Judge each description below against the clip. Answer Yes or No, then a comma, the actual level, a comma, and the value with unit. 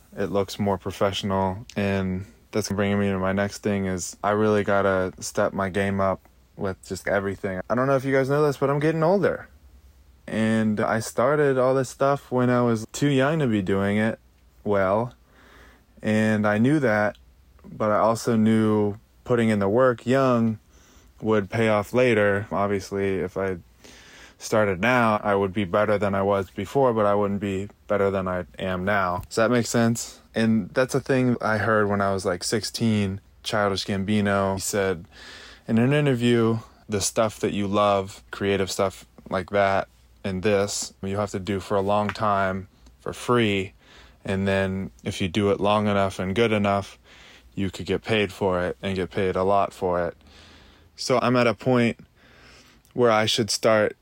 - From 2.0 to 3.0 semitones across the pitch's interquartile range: Yes, narrow, 2.6 semitones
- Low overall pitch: Yes, low, 100 Hz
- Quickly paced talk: No, average, 185 wpm